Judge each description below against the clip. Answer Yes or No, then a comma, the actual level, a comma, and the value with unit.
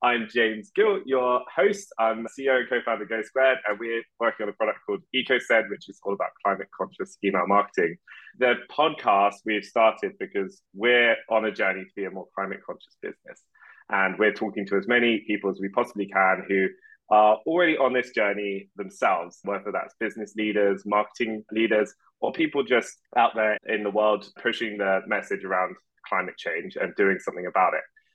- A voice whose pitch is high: No, low, 110 Hz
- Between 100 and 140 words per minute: No, average, 190 wpm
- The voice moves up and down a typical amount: Yes, average, 3.2 semitones